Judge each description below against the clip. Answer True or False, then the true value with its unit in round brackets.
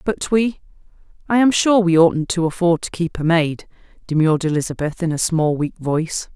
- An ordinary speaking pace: True (180 wpm)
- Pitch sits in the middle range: True (170 Hz)